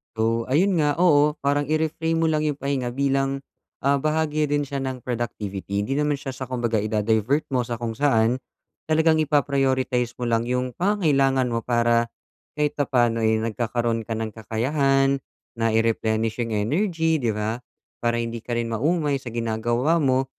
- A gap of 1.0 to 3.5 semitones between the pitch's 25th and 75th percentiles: No, average, 4.1 semitones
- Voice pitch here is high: No, low, 130 Hz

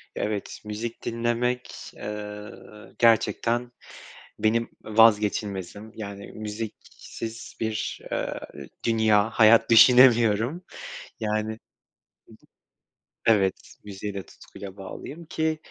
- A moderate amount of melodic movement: No, narrow, 2.0 semitones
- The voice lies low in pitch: Yes, low, 110 Hz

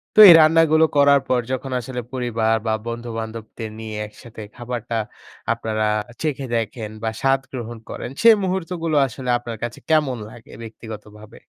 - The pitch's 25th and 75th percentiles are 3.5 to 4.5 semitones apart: Yes, average, 4.0 semitones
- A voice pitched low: Yes, low, 120 Hz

